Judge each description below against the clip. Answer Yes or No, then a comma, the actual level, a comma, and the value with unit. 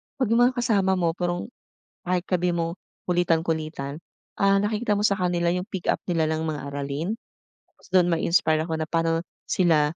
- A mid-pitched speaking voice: Yes, medium, 175 Hz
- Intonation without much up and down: No, average, 3.0 semitones